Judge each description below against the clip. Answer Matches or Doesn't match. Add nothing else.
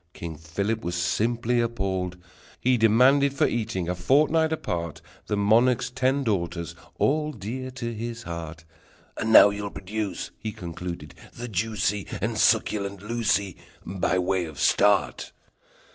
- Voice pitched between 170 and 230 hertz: Doesn't match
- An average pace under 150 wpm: Matches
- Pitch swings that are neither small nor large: Matches